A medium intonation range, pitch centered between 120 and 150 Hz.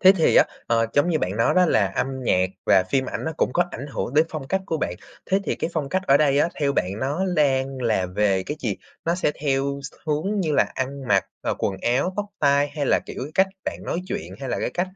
Yes: average, 4.9 semitones; medium, 140 Hz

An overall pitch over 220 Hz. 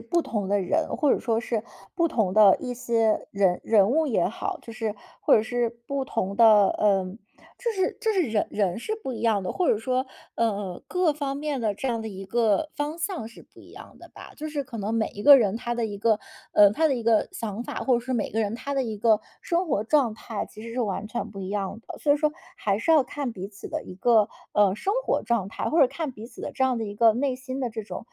Yes: high, 230 Hz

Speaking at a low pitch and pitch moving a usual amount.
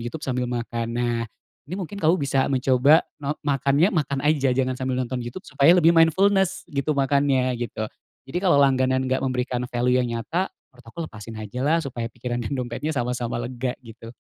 Yes: low, 130 Hz; average, 3.2 semitones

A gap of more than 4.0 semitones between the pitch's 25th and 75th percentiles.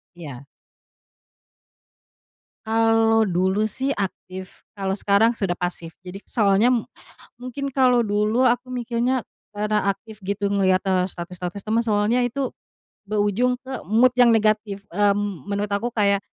No: average, 3.2 semitones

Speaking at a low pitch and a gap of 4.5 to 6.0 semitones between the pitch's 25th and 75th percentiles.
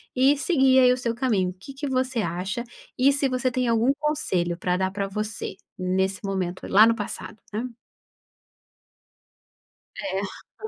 No: high, 230 Hz; wide, 5.4 semitones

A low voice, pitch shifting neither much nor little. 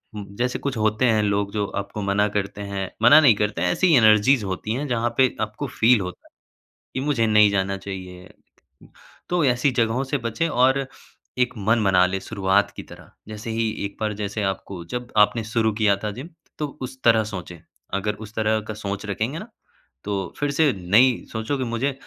Yes: low, 110 Hz; average, 3.7 semitones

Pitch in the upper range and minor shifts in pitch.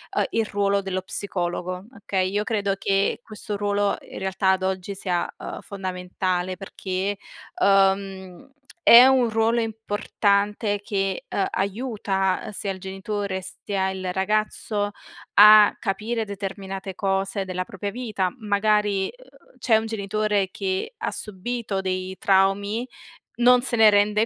Yes: high, 200 Hz; narrow, 1.9 semitones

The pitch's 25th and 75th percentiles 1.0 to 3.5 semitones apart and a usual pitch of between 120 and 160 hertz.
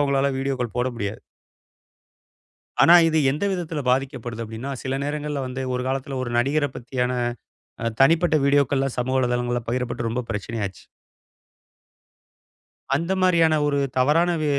Yes: average, 3.2 semitones; low, 135 Hz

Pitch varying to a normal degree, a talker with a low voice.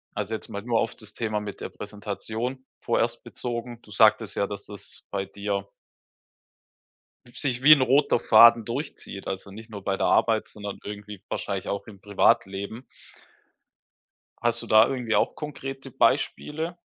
Yes: average, 3.2 semitones; low, 110 Hz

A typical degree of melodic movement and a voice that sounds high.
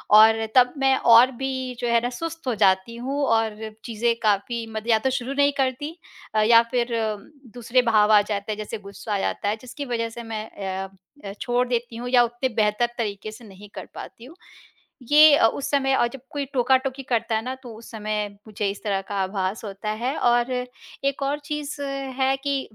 Yes: average, 3.5 semitones; high, 235 Hz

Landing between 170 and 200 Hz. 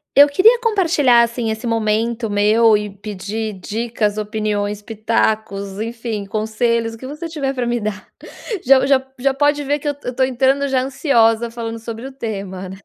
No: high, 230 Hz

